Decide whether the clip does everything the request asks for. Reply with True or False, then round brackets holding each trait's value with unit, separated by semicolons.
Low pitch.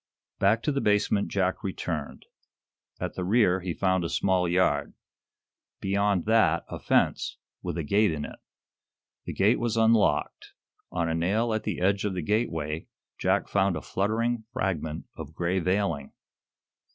True (95 Hz)